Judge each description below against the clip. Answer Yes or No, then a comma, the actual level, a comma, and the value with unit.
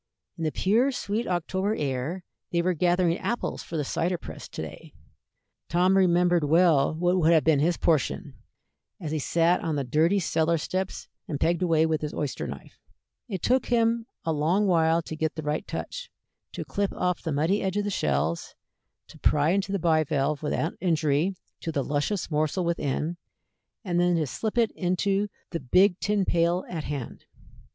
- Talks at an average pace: Yes, average, 180 wpm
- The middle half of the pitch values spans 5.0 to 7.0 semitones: No, average, 3.4 semitones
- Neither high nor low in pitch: Yes, medium, 170 Hz